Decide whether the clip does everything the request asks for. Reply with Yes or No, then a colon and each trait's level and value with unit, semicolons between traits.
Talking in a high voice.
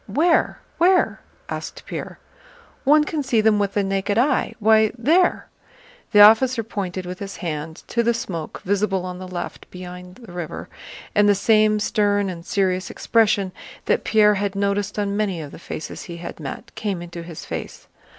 Yes: high, 200 Hz